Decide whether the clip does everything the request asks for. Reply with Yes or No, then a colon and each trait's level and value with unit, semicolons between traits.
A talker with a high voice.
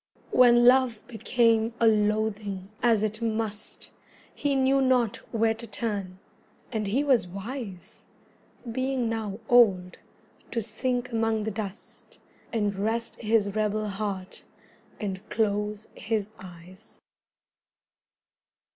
Yes: high, 220 Hz